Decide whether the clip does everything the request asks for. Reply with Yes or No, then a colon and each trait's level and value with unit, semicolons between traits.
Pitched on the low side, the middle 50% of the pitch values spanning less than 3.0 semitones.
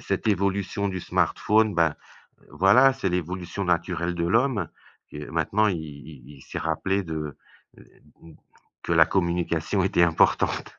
No: very low, 90 Hz; average, 3.4 semitones